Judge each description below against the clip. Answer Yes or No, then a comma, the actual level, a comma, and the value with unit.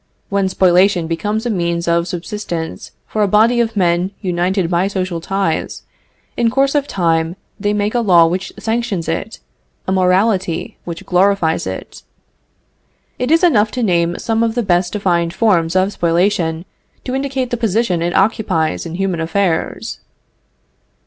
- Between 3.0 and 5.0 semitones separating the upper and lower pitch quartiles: Yes, average, 4.2 semitones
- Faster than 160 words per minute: No, average, 155 wpm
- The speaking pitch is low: No, high, 190 Hz